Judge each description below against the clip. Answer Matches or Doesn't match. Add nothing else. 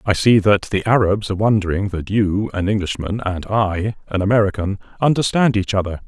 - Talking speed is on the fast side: Doesn't match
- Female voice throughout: Doesn't match